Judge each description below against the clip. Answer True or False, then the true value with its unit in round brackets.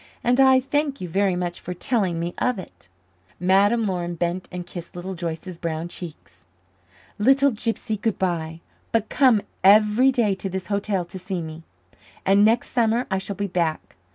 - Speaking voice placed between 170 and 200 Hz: True (190 Hz)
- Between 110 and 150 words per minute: False (175 wpm)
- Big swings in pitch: False (4.3 semitones)